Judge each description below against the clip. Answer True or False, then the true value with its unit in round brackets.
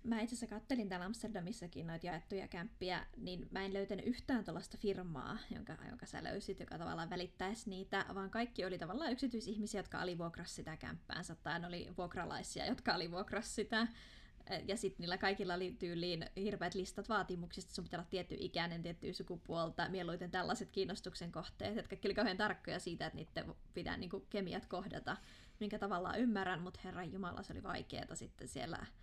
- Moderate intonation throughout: True (3.0 semitones)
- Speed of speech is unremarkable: False (165 wpm)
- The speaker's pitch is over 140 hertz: True (190 Hz)